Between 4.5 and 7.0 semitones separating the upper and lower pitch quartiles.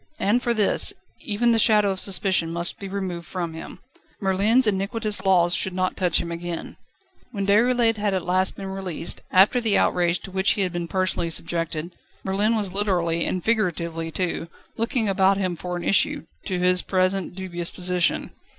No: average, 2.7 semitones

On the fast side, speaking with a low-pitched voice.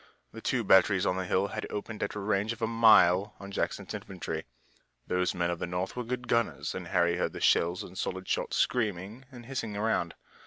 Yes: fast, 210 wpm; low, 100 Hz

